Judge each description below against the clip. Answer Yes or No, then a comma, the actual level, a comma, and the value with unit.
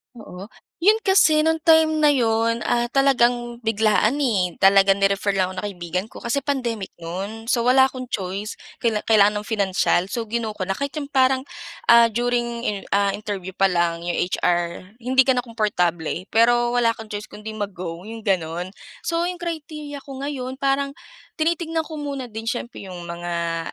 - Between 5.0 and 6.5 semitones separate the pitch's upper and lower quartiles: Yes, wide, 5.4 semitones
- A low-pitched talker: No, high, 225 Hz